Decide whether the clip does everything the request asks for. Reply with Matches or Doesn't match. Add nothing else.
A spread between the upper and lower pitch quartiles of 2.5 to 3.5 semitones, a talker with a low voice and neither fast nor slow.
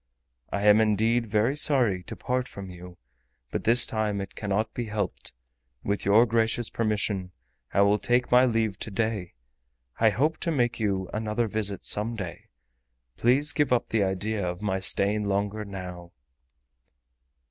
Matches